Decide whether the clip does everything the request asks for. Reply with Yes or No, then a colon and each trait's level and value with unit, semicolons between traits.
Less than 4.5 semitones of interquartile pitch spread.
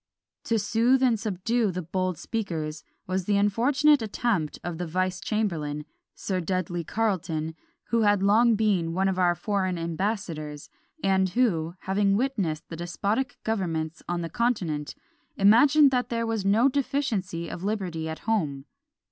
No: average, 4.8 semitones